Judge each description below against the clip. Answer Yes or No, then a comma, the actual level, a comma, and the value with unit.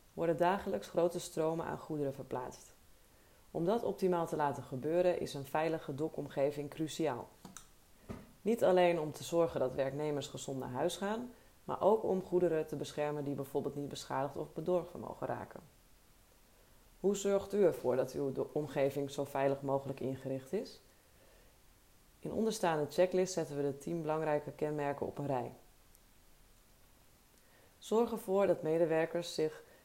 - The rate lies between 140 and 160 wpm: Yes, average, 145 wpm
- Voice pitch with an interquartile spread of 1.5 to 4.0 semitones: Yes, average, 3.7 semitones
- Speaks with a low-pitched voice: No, medium, 155 Hz